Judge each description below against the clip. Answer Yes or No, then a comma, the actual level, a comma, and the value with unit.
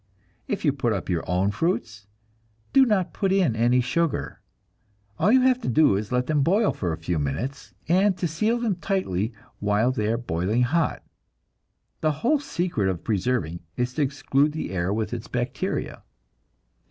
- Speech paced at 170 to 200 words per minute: Yes, average, 175 wpm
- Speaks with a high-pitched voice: No, low, 130 Hz